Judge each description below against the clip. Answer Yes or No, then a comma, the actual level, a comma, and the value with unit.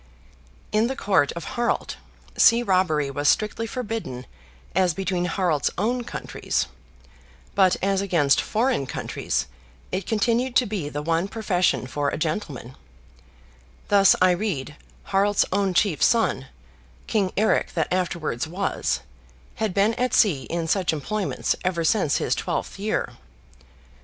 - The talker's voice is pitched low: No, high, 190 Hz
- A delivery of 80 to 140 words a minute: Yes, slow, 135 wpm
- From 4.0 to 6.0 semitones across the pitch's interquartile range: Yes, average, 5.0 semitones